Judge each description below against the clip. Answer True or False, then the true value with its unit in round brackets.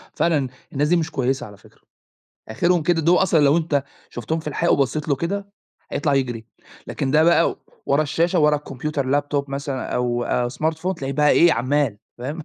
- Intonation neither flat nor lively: True (3.3 semitones)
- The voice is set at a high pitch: False (145 Hz)